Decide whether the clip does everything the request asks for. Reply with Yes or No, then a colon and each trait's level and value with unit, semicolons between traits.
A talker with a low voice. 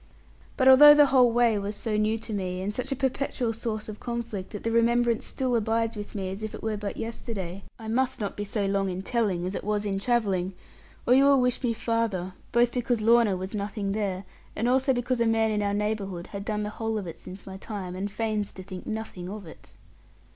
No: high, 215 Hz